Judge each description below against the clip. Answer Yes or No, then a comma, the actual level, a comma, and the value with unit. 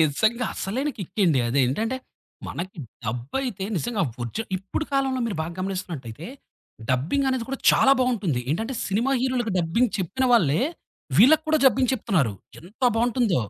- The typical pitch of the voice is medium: No, high, 215 Hz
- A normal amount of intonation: No, wide, 7.6 semitones